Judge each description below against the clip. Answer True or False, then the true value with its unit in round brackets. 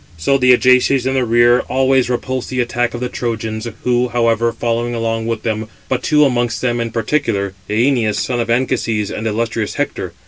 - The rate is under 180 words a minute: False (185 wpm)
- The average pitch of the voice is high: False (120 Hz)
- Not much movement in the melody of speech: True (2.0 semitones)